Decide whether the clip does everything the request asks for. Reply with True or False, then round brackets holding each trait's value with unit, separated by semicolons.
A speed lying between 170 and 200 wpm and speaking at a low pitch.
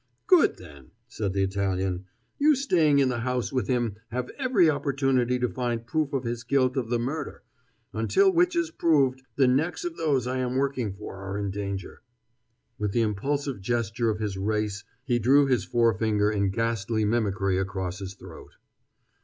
True (175 wpm; 120 Hz)